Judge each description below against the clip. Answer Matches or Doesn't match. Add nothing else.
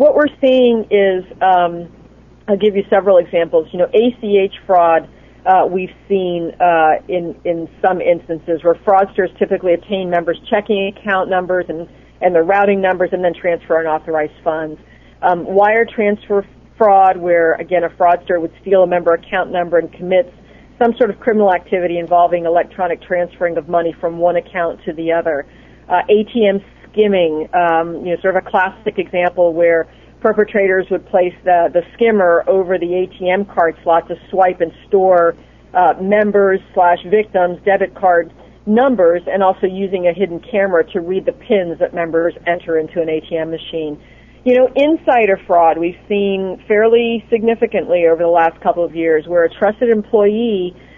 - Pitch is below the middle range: Doesn't match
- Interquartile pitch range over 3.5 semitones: Doesn't match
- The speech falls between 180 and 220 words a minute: Doesn't match